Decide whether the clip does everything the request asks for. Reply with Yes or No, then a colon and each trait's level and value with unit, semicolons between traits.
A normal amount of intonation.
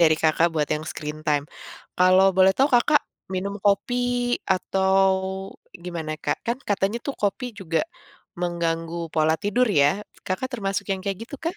Yes: average, 3.8 semitones